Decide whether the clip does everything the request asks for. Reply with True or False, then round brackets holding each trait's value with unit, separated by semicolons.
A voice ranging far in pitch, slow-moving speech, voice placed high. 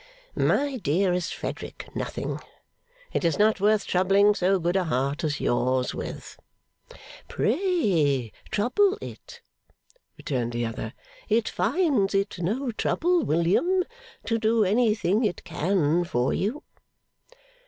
True (6.3 semitones; 120 wpm; 195 Hz)